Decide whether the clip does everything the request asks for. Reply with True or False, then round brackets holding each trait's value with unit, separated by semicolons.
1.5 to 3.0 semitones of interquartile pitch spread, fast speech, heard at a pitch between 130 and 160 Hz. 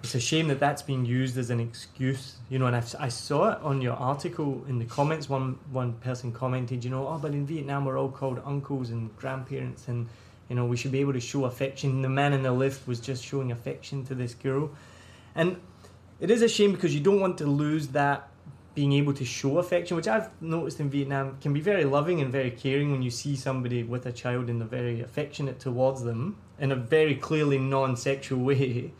True (2.4 semitones; 230 wpm; 135 Hz)